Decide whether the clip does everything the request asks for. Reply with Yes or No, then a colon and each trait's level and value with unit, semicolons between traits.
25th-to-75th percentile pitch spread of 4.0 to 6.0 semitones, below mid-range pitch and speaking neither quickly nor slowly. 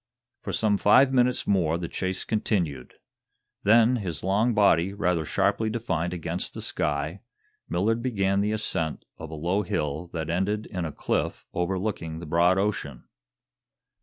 Yes: average, 4.3 semitones; very low, 95 Hz; average, 150 wpm